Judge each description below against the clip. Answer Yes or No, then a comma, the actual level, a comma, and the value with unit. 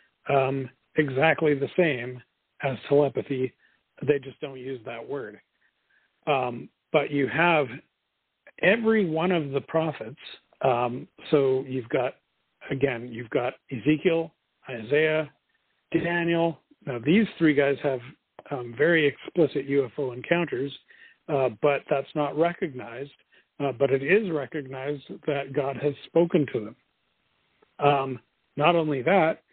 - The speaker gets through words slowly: Yes, slow, 125 wpm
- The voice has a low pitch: No, medium, 145 Hz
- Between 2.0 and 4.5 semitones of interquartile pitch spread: Yes, average, 3.3 semitones